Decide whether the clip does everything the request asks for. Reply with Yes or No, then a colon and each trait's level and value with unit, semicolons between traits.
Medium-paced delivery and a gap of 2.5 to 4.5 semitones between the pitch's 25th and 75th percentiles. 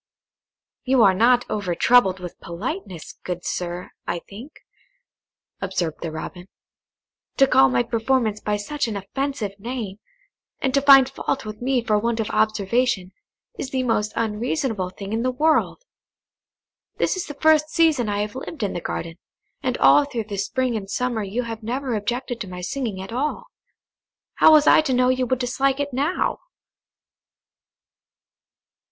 No: average, 160 wpm; average, 5.0 semitones